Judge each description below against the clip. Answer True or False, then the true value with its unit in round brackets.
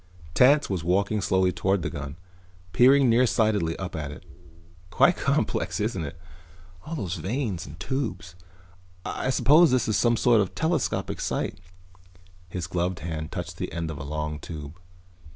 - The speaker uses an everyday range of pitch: False (6.4 semitones)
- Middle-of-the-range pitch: False (90 Hz)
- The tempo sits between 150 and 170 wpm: True (160 wpm)